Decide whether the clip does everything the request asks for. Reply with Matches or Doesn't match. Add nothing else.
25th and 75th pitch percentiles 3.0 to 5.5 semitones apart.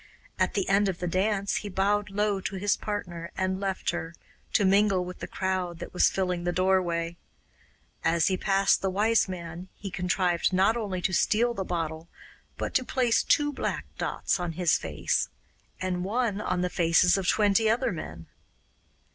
Doesn't match